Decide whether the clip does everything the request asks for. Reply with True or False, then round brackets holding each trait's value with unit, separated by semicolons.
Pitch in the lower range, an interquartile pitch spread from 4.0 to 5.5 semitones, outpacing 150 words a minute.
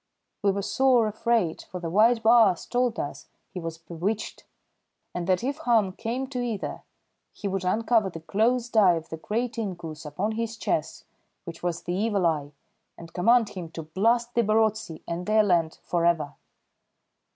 False (200 Hz; 5.1 semitones; 175 wpm)